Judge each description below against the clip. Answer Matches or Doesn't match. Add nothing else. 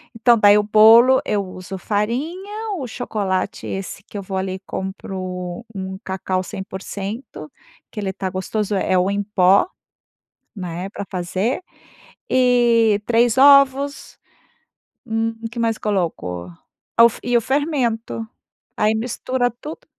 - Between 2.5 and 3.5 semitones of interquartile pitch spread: Doesn't match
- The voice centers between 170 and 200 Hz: Doesn't match